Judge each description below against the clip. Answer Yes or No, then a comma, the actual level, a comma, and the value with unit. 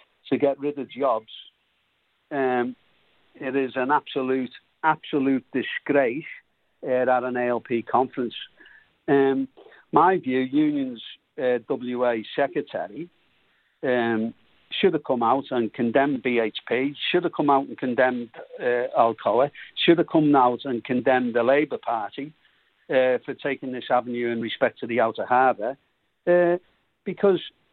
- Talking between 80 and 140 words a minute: Yes, slow, 135 wpm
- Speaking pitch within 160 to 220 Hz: No, low, 130 Hz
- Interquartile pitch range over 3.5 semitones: No, average, 3.0 semitones